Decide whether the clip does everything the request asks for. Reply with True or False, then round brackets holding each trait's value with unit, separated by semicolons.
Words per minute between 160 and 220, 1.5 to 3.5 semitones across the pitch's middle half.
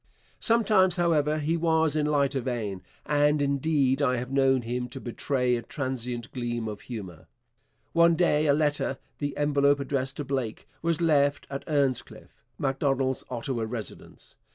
False (150 wpm; 3.1 semitones)